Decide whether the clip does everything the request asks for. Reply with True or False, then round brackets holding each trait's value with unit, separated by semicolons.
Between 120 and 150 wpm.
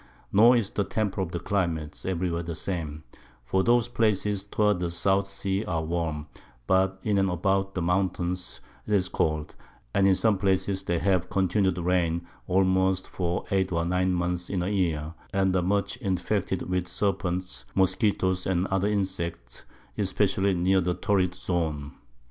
False (160 wpm)